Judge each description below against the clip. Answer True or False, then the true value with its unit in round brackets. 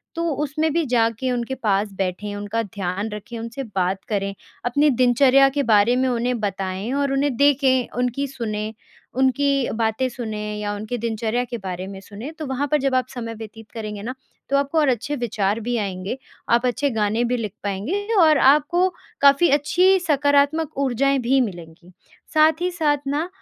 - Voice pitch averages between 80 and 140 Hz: False (245 Hz)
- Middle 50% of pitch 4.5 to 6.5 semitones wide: True (4.9 semitones)